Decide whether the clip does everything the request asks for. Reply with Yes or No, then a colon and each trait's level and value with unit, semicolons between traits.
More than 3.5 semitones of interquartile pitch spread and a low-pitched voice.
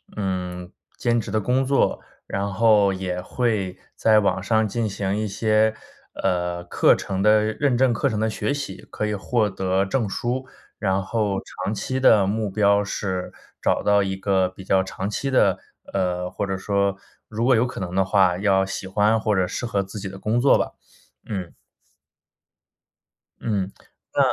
No: narrow, 2.5 semitones; low, 100 Hz